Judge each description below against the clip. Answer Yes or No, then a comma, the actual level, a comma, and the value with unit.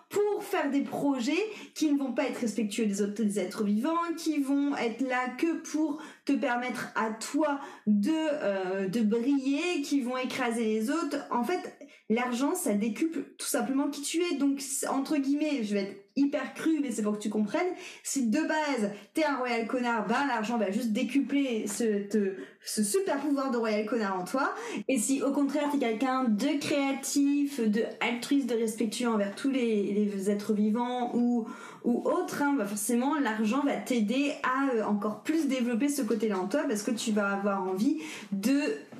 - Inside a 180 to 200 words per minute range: Yes, average, 190 wpm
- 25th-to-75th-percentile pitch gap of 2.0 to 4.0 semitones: No, average, 4.6 semitones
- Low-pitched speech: No, very high, 255 Hz